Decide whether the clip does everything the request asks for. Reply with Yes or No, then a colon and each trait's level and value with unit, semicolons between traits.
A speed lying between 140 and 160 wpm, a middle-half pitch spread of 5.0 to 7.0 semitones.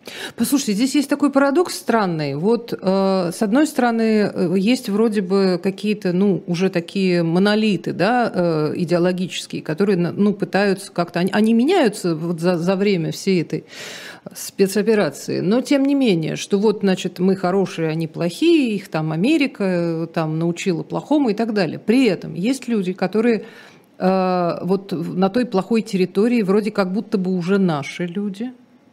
No: average, 155 wpm; average, 4.1 semitones